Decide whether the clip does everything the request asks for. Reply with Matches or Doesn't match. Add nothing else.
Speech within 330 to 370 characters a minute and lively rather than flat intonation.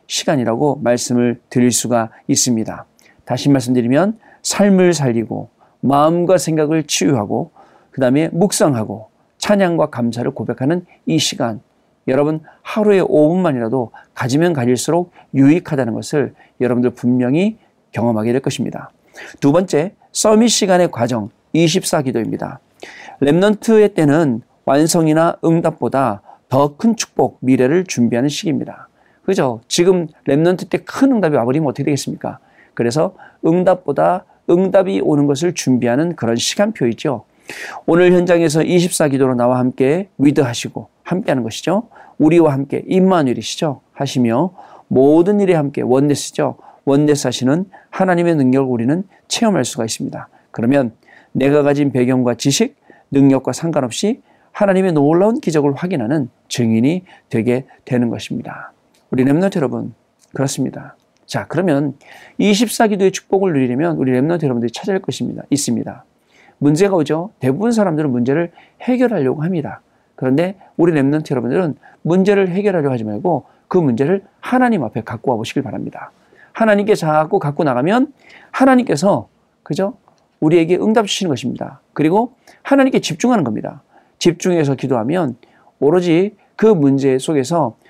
Matches